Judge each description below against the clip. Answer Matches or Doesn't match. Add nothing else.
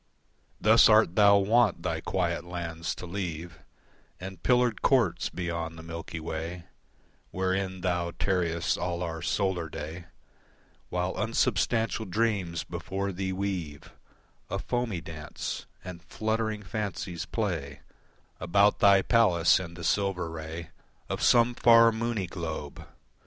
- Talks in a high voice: Doesn't match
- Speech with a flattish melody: Doesn't match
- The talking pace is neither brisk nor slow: Doesn't match